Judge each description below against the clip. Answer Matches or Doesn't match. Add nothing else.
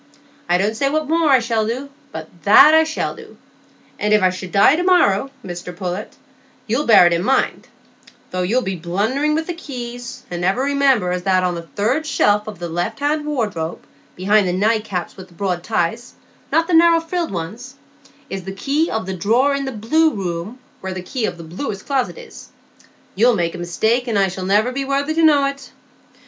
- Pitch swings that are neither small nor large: Doesn't match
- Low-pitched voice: Doesn't match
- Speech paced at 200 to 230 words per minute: Matches